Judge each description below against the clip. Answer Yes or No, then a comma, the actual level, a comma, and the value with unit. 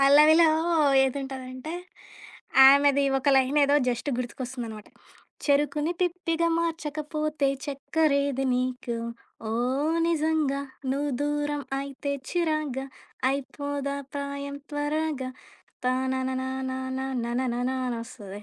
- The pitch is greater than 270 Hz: Yes, very high, 280 Hz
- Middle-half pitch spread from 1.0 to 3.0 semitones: Yes, narrow, 2.5 semitones